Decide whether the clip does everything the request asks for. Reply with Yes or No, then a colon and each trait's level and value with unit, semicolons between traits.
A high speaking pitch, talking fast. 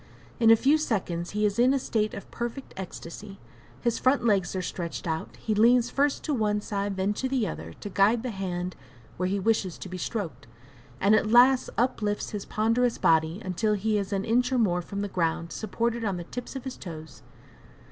Yes: high, 210 Hz; fast, 210 wpm